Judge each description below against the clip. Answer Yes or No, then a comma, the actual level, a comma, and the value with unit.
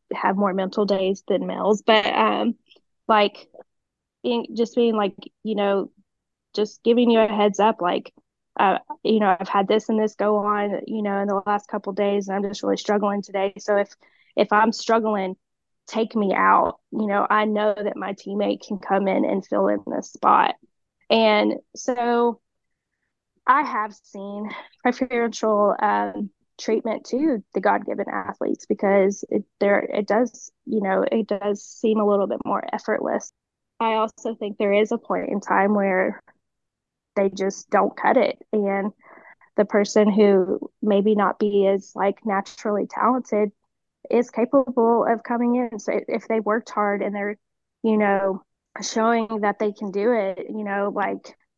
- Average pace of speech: Yes, average, 170 wpm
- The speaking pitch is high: Yes, high, 210 Hz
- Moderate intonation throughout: No, narrow, 2.0 semitones